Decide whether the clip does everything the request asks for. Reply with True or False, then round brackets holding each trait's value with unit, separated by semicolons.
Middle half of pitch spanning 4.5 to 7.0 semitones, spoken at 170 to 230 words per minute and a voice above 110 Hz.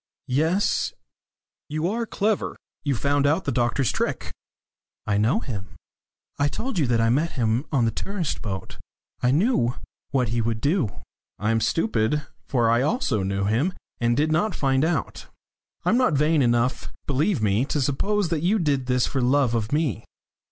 True (5.6 semitones; 175 wpm; 135 Hz)